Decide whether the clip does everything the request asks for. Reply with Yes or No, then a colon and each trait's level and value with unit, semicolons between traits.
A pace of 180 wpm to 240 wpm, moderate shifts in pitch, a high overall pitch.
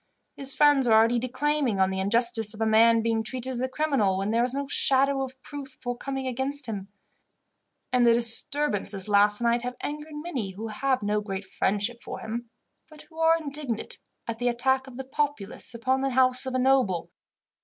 Yes: average, 195 wpm; average, 3.5 semitones; high, 245 Hz